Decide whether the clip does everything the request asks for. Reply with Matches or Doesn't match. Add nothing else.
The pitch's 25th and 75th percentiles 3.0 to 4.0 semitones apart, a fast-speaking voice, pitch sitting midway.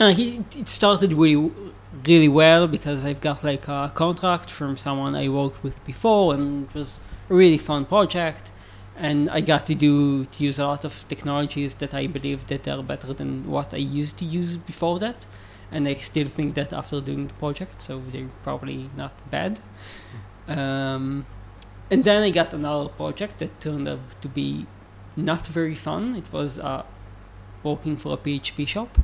Matches